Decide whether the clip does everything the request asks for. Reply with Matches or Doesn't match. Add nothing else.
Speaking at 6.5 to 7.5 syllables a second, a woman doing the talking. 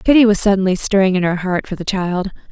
Doesn't match